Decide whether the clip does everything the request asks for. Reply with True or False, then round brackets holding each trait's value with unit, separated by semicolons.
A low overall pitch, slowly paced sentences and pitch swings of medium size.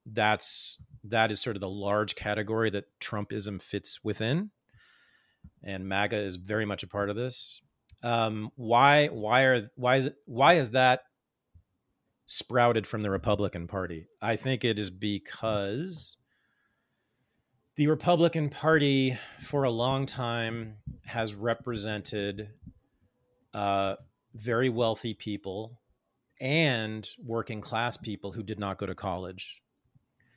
True (110 Hz; 125 wpm; 3.8 semitones)